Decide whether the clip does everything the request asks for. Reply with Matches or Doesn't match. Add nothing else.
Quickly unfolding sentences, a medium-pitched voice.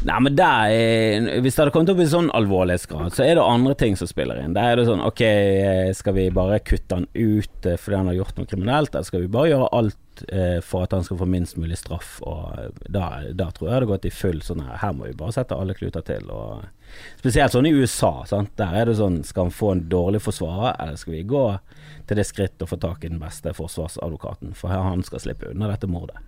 Doesn't match